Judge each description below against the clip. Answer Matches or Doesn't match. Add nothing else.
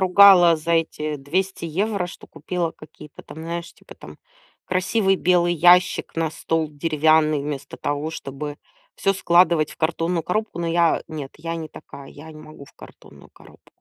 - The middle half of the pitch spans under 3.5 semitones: Matches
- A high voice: Doesn't match